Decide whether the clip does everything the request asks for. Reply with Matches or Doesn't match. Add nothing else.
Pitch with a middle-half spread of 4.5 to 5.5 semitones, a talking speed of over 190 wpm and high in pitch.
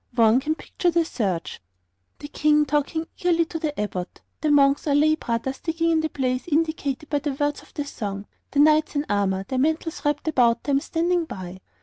Doesn't match